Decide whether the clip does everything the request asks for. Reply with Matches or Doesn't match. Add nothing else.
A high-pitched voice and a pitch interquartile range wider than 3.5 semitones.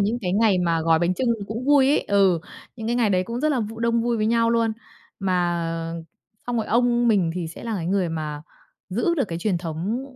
Matches